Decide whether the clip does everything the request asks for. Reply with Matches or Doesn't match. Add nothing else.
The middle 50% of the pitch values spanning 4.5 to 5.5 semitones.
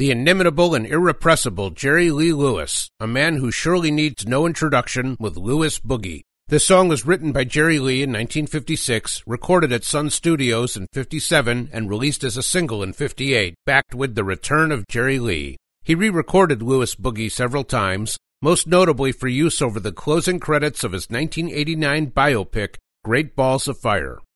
Matches